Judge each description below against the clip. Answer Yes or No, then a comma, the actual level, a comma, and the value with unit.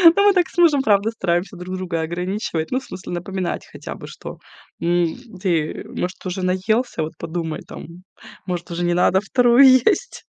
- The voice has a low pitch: No, medium, 185 Hz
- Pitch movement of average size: Yes, average, 4.7 semitones